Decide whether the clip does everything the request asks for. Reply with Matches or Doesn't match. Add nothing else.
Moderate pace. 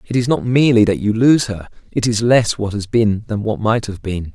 Doesn't match